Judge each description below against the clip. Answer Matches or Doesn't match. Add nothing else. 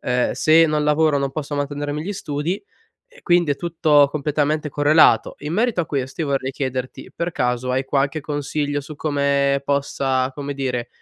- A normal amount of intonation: Doesn't match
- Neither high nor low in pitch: Matches